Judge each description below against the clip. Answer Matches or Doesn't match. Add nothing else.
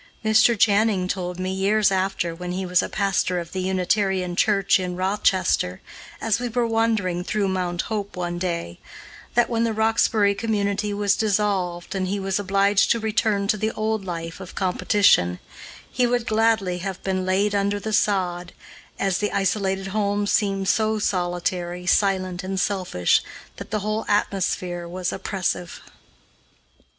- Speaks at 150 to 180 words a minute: Matches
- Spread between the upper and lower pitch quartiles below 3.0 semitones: Matches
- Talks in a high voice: Matches